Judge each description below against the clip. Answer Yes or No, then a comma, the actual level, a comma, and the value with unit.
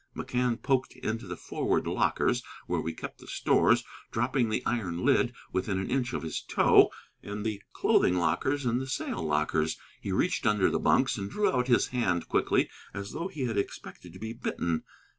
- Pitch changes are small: No, wide, 5.5 semitones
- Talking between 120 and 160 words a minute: No, average, 190 wpm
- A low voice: Yes, low, 110 Hz